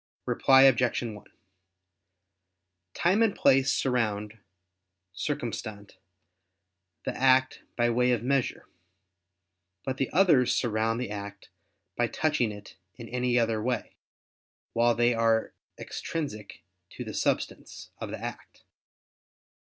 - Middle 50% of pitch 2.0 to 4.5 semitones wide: Yes, average, 3.3 semitones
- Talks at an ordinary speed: No, slow, 115 wpm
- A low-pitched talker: Yes, low, 120 Hz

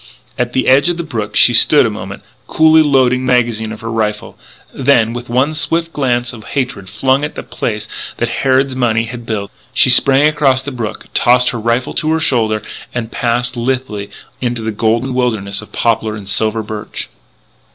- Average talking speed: Yes, average, 190 wpm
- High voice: No, low, 120 Hz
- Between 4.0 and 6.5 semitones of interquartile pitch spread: No, average, 3.0 semitones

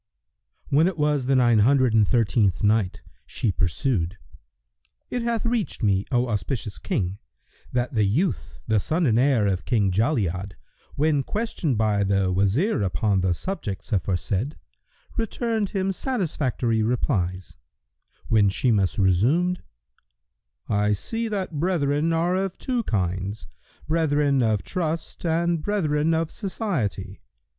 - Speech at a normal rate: No, slow, 130 wpm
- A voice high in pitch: No, low, 125 Hz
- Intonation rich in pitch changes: Yes, wide, 8.6 semitones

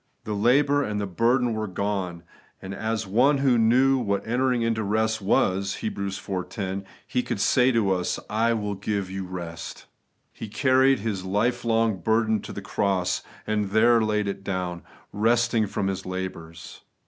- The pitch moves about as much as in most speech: Yes, average, 3.2 semitones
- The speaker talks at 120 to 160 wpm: No, average, 170 wpm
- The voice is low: Yes, low, 105 Hz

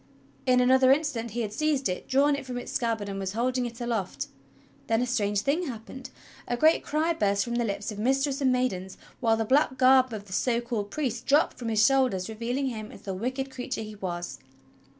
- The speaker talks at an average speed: No, fast, 215 wpm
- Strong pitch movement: No, average, 3.7 semitones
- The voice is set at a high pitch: Yes, high, 240 Hz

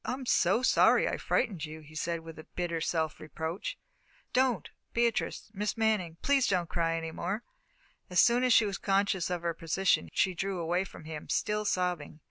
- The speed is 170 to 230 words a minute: Yes, average, 180 wpm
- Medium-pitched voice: Yes, medium, 180 Hz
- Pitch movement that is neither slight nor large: Yes, average, 4.4 semitones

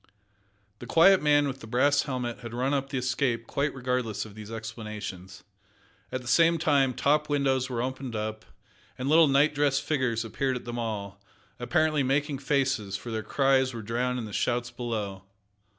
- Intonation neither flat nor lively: Yes, average, 3.5 semitones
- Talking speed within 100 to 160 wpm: No, average, 180 wpm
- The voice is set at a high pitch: No, low, 125 Hz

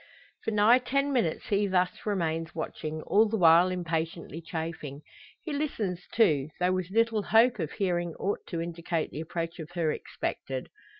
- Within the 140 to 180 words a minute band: Yes, average, 165 wpm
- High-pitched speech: No, medium, 175 Hz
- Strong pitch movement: No, average, 4.5 semitones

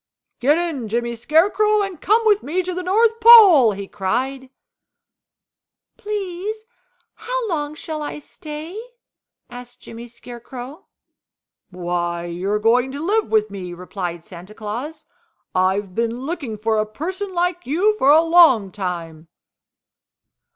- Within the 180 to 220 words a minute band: No, slow, 135 wpm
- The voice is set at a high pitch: Yes, very high, 270 Hz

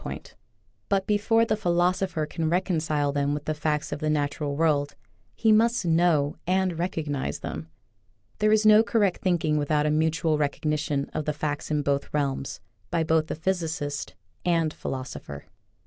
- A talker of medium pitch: Yes, medium, 155 Hz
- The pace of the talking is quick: No, average, 170 wpm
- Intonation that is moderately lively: Yes, average, 3.6 semitones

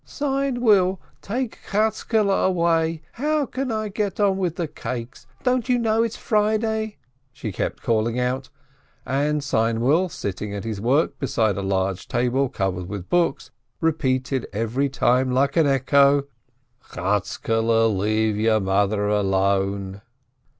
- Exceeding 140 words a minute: No, slow, 135 wpm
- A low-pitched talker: Yes, low, 130 Hz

